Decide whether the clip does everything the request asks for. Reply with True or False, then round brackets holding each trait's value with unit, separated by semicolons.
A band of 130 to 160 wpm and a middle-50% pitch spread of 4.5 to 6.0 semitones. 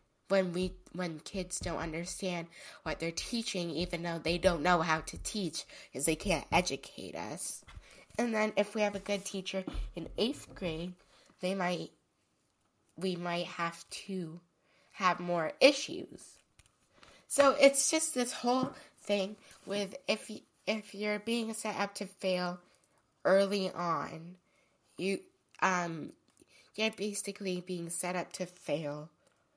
False (140 wpm; 2.9 semitones)